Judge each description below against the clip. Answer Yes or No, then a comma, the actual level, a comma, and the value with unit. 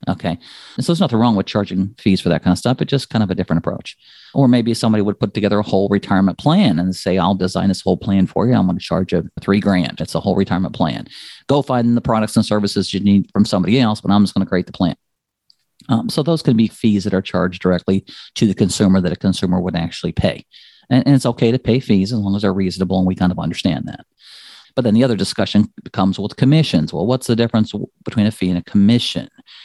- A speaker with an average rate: No, fast, 255 wpm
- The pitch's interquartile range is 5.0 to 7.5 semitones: No, average, 3.3 semitones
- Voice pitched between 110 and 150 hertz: No, low, 100 Hz